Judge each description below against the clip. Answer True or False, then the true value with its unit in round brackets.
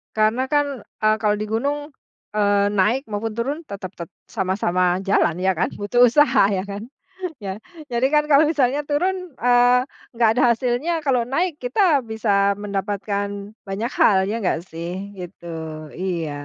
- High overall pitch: True (220 Hz)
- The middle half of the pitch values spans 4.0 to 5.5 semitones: True (4.6 semitones)